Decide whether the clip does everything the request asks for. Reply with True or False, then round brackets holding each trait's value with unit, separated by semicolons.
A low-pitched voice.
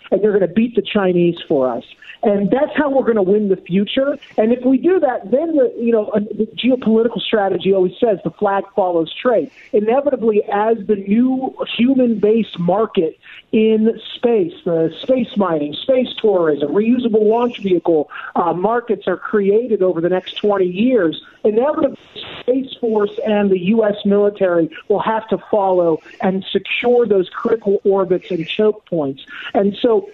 False (210 Hz)